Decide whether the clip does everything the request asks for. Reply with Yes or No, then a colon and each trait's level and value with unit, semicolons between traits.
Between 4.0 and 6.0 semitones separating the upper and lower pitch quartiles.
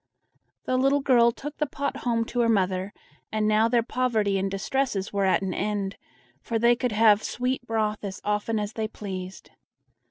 No: average, 3.3 semitones